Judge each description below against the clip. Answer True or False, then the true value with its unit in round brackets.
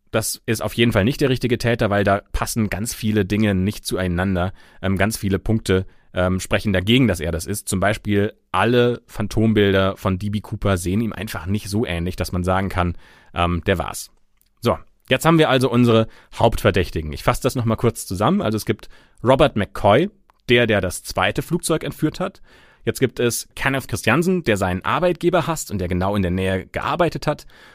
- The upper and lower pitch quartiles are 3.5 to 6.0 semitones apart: True (4.2 semitones)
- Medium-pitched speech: False (105 Hz)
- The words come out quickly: True (195 wpm)